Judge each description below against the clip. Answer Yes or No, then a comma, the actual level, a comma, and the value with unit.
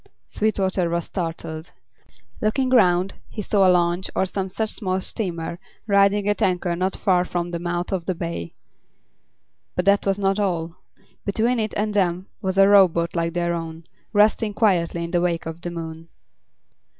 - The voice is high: No, medium, 180 Hz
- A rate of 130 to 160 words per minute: No, average, 170 wpm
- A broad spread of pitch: No, average, 2.8 semitones